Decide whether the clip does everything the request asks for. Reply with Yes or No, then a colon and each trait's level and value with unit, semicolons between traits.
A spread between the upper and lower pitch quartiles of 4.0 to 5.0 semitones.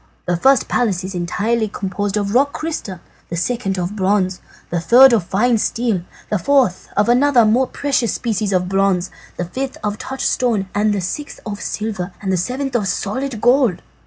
Yes: average, 4.7 semitones